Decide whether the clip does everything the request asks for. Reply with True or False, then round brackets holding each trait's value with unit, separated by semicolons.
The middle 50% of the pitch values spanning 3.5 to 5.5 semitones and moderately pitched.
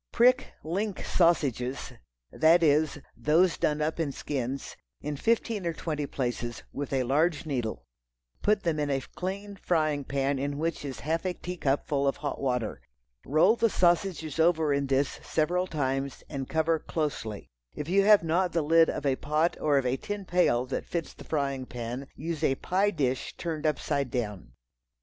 True (3.9 semitones; 150 Hz)